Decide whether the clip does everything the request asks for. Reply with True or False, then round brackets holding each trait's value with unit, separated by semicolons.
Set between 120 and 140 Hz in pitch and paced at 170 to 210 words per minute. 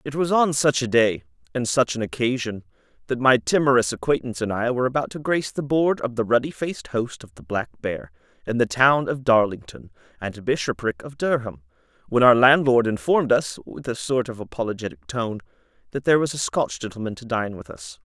True (125 Hz; 200 wpm)